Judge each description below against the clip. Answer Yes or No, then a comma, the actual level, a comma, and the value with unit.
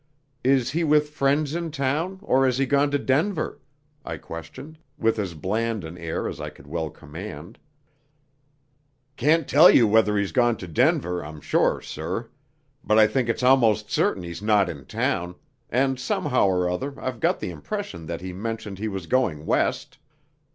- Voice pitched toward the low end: Yes, low, 110 Hz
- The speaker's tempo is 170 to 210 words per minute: Yes, average, 175 wpm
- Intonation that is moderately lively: No, wide, 7.3 semitones